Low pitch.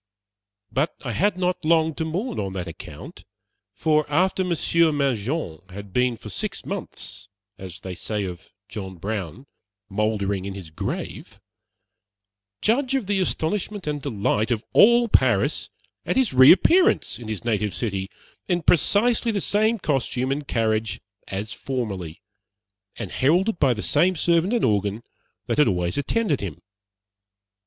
Yes: low, 130 Hz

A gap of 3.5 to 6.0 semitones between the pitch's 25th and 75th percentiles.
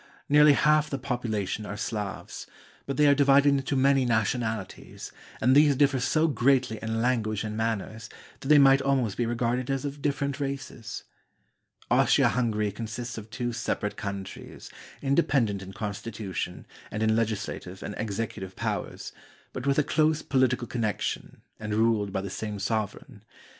Yes: average, 4.4 semitones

